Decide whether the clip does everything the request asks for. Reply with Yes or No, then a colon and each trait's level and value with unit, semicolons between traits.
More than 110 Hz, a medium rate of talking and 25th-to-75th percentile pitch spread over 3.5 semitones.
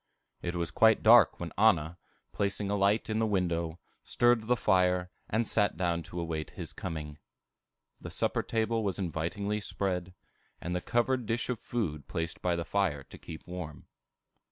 No: very low, 95 Hz; average, 170 wpm; average, 4.4 semitones